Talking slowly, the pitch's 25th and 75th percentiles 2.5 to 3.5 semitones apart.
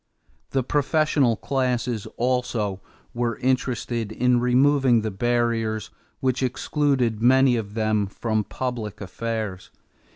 Yes: slow, 105 wpm; average, 2.8 semitones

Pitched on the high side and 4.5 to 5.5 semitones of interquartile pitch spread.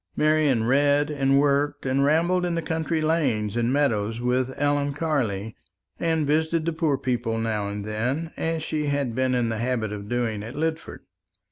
No: medium, 140 Hz; average, 5.2 semitones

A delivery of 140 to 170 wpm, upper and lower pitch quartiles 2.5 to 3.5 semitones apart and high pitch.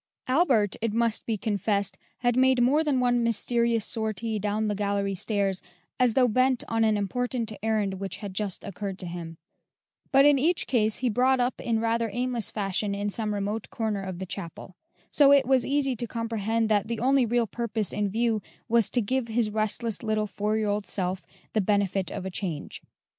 No: average, 195 wpm; average, 3.1 semitones; high, 220 Hz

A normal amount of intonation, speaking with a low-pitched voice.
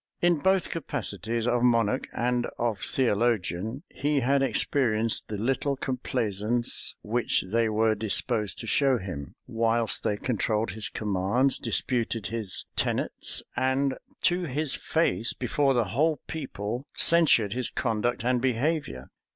Yes: average, 3.8 semitones; low, 120 Hz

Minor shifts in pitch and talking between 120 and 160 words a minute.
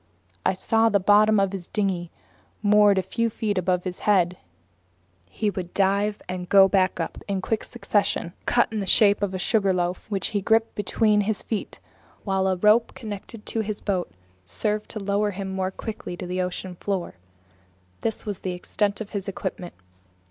No: narrow, 2.3 semitones; average, 190 wpm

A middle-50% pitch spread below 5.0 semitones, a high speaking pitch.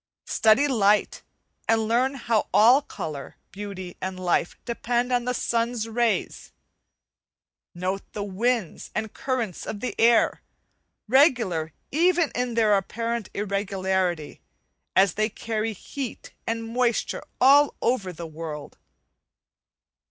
Yes: average, 4.2 semitones; high, 225 Hz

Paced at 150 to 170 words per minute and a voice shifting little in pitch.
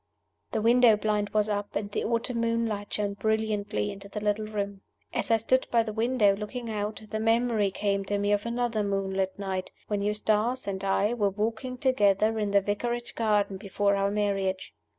No: average, 185 wpm; narrow, 2.1 semitones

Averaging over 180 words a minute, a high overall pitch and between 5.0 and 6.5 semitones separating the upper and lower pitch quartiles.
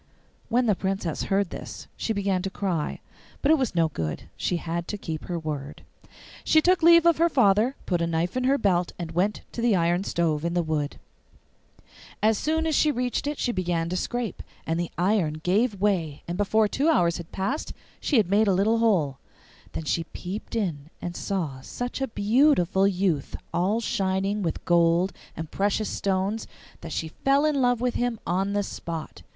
Yes: average, 195 wpm; high, 195 Hz; average, 5.3 semitones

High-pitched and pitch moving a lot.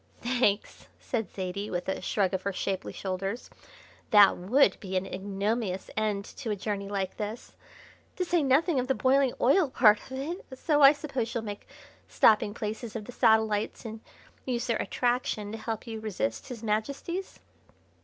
No: high, 220 Hz; average, 4.2 semitones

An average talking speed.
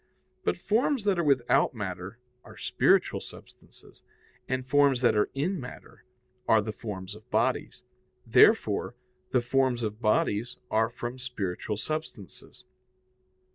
No: slow, 130 wpm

